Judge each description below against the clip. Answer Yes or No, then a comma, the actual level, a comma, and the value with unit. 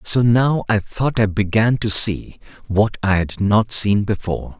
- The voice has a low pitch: Yes, low, 105 Hz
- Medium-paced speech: Yes, average, 185 wpm